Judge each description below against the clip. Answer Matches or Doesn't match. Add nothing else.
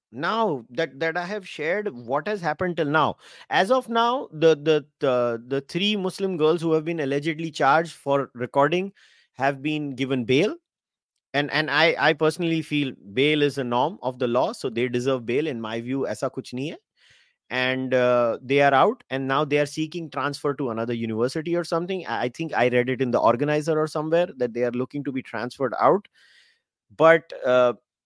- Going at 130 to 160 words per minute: Doesn't match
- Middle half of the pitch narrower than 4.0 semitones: Doesn't match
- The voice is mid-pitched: Matches